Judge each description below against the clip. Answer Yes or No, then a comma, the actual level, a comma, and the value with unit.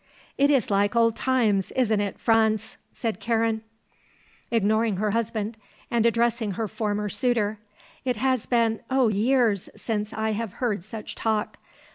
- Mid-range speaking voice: No, high, 225 Hz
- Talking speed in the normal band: Yes, average, 145 wpm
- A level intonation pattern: Yes, narrow, 1.9 semitones